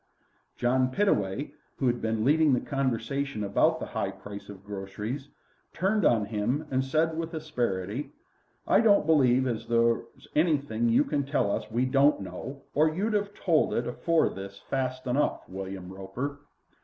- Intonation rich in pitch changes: Yes, wide, 5.9 semitones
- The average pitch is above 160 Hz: No, low, 130 Hz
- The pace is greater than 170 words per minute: No, average, 165 wpm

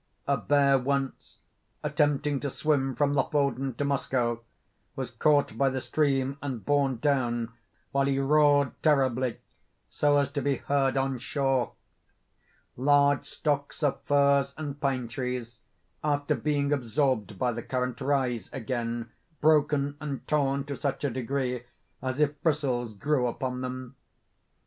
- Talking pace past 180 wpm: No, average, 140 wpm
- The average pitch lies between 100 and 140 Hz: Yes, low, 135 Hz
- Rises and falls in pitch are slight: Yes, narrow, 2.1 semitones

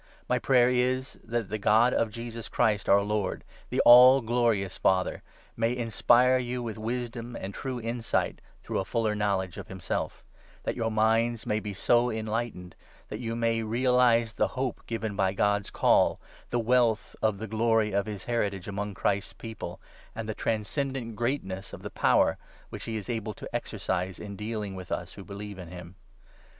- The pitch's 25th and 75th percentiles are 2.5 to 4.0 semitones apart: Yes, average, 2.8 semitones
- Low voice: Yes, low, 110 Hz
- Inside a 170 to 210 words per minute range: Yes, average, 185 wpm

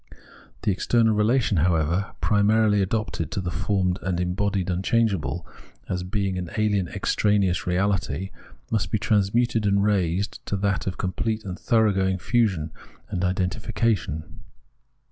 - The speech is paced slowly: Yes, slow, 130 wpm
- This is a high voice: No, low, 100 Hz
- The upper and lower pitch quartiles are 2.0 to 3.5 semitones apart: Yes, average, 2.8 semitones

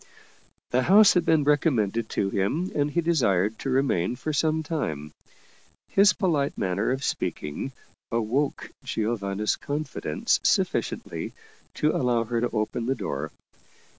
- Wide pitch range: Yes, wide, 6.1 semitones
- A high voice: No, low, 125 Hz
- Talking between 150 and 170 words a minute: No, slow, 135 wpm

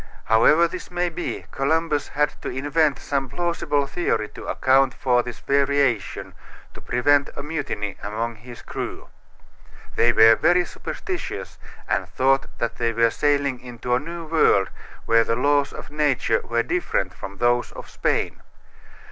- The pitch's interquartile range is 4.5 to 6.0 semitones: No, average, 4.1 semitones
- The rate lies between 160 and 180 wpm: No, average, 150 wpm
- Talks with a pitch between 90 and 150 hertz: Yes, low, 135 Hz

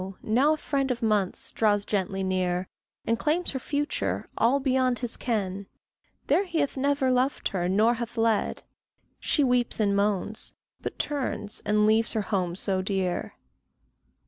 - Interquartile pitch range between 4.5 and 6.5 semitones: Yes, average, 4.9 semitones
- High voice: Yes, high, 225 Hz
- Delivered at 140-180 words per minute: Yes, average, 155 wpm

